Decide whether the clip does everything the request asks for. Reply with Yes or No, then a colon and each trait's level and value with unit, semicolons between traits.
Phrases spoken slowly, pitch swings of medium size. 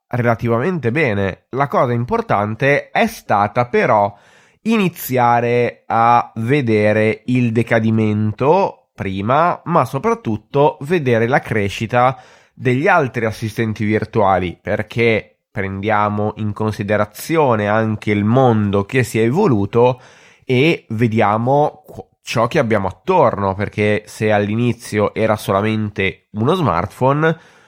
Yes: slow, 100 wpm; average, 3.1 semitones